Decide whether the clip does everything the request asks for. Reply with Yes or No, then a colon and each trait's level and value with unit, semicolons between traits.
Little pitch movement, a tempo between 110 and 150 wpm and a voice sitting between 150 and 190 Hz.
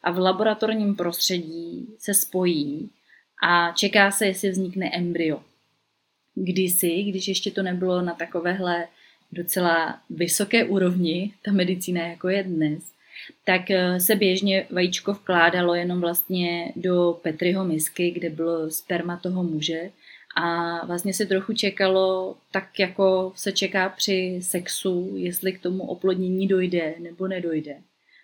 Yes: narrow, 1.9 semitones; average, 125 wpm; medium, 185 Hz